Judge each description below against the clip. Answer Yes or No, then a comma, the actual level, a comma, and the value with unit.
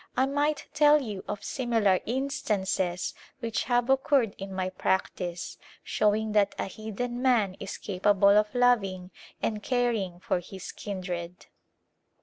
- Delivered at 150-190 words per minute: No, slow, 135 wpm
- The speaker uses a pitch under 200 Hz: No, high, 210 Hz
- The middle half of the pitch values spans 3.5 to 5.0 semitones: Yes, average, 4.5 semitones